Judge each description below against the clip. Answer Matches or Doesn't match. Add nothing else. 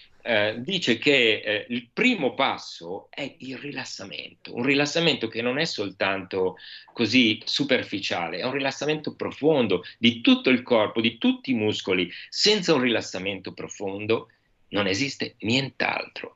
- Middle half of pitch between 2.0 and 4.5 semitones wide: Doesn't match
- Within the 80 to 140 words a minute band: Matches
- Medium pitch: Doesn't match